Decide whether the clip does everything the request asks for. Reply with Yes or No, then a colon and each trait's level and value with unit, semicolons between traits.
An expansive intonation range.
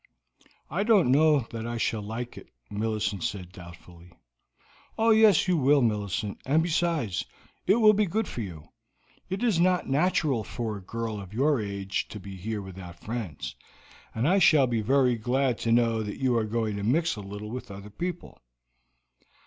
Yes: wide, 7.0 semitones